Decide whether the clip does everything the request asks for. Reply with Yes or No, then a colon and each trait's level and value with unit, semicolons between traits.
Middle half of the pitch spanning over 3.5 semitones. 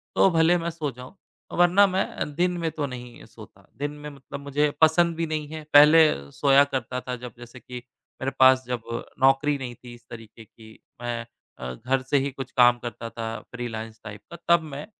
Yes: average, 4.1 semitones